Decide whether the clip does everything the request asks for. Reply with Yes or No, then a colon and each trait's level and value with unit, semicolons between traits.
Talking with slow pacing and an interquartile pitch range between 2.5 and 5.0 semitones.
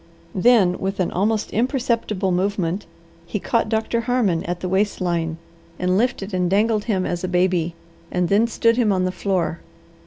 No: average, 175 wpm; average, 3.5 semitones